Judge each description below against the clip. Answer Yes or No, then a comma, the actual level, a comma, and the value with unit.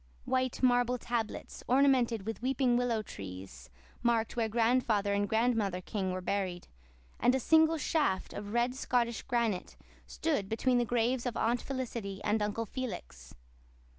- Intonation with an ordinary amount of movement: Yes, average, 3.5 semitones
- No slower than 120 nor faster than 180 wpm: Yes, average, 145 wpm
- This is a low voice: No, high, 235 Hz